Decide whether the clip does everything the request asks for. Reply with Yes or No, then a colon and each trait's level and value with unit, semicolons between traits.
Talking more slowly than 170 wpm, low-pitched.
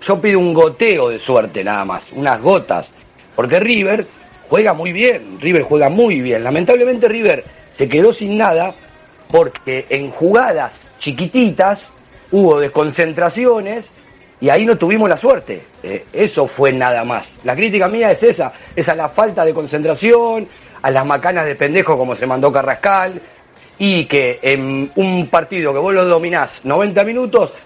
No: average, 160 wpm; high, 190 Hz